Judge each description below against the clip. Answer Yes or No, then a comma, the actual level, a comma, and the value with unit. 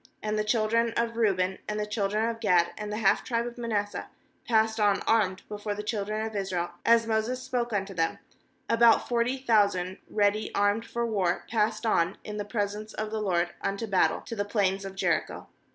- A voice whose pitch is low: No, high, 210 Hz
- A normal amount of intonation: No, narrow, 2.3 semitones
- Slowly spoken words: No, average, 195 wpm